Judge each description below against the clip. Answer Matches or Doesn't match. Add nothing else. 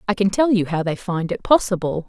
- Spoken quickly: Matches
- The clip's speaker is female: Matches